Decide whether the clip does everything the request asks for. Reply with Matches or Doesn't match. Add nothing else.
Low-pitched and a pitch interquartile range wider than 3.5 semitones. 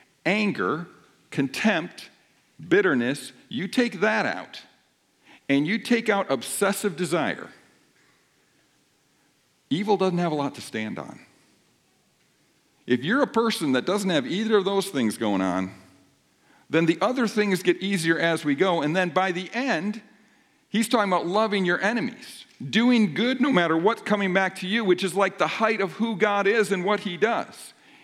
Doesn't match